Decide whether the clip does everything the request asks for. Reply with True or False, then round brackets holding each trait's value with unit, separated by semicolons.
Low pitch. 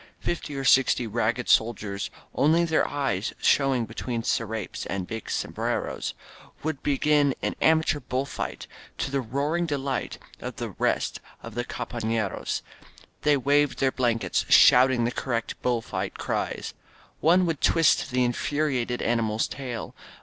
True (130 Hz)